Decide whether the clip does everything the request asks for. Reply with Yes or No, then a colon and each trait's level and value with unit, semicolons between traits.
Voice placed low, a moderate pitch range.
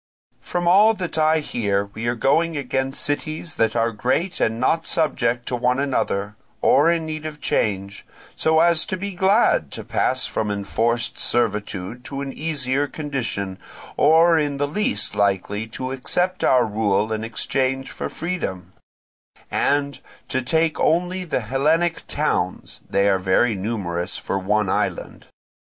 No: low, 130 Hz; wide, 6.8 semitones